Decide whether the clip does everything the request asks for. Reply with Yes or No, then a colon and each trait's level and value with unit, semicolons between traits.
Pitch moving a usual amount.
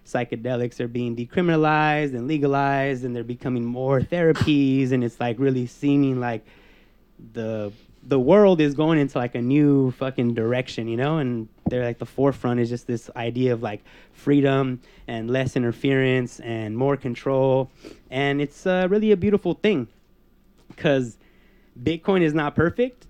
Yes: average, 3.3 semitones